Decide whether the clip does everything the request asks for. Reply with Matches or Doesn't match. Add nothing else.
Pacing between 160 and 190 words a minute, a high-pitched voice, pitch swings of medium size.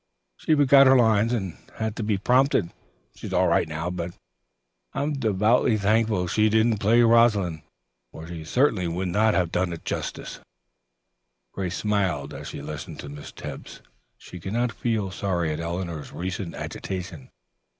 Doesn't match